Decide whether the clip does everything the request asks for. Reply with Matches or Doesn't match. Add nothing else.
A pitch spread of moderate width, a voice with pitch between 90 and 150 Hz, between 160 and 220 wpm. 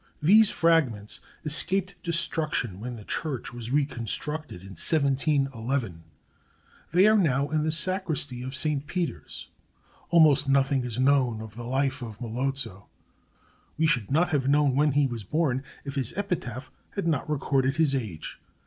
Doesn't match